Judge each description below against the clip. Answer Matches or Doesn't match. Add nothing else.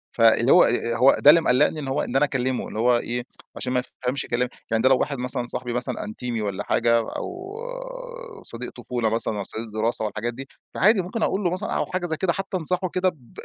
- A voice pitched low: Matches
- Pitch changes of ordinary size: Doesn't match